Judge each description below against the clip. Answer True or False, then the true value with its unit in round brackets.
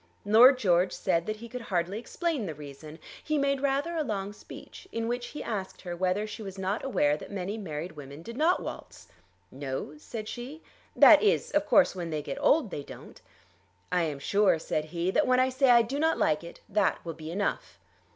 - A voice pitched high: True (205 Hz)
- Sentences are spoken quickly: True (210 wpm)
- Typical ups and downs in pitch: False (7.1 semitones)